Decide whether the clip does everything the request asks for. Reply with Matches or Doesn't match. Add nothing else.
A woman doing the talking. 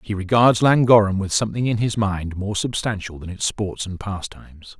Doesn't match